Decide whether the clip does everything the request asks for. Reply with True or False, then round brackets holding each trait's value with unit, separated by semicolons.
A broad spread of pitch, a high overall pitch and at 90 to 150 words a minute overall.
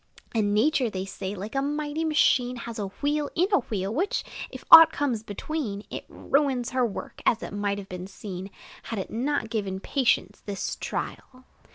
False (6.2 semitones; 230 Hz; 185 wpm)